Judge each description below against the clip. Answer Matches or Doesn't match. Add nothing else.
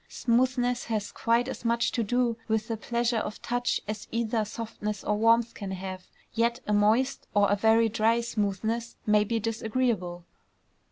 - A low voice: Doesn't match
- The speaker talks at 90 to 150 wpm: Doesn't match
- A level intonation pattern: Matches